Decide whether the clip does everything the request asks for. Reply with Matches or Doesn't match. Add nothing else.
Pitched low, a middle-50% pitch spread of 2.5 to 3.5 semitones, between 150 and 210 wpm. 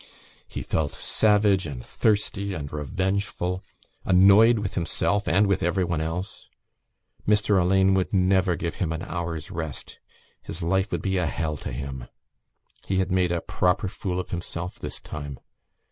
Matches